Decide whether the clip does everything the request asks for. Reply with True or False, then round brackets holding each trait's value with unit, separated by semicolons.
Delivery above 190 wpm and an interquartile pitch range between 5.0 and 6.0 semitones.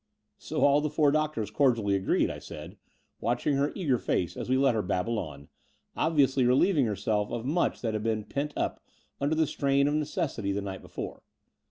True (200 wpm; 5.6 semitones)